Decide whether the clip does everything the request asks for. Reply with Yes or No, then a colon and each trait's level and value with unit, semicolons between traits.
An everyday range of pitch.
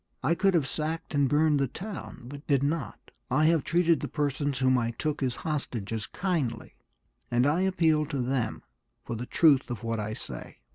Yes: average, 4.4 semitones